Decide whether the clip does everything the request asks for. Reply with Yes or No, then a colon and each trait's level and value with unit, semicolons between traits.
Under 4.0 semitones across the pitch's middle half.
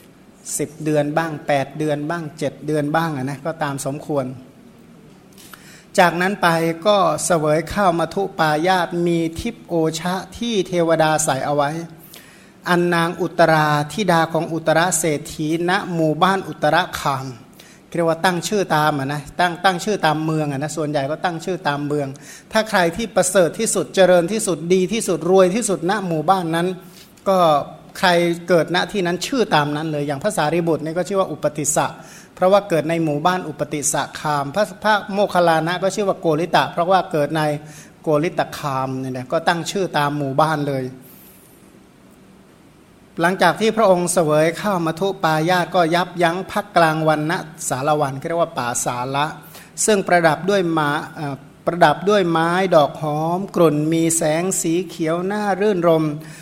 Yes: average, 3.2 semitones